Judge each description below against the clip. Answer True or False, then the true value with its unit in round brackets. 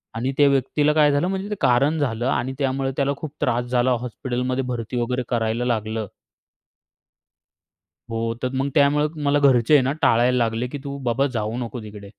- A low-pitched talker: True (125 Hz)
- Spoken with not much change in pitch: False (3.2 semitones)